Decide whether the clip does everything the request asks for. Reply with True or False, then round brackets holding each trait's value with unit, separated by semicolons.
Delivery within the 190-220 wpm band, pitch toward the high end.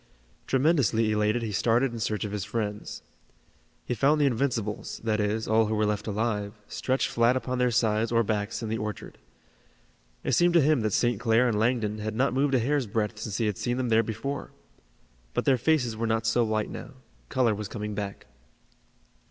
False (200 wpm; 115 Hz)